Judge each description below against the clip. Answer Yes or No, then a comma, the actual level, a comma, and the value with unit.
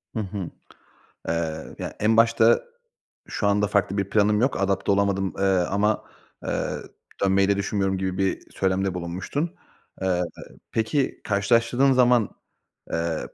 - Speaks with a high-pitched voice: No, low, 100 Hz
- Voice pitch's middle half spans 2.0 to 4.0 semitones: Yes, average, 2.7 semitones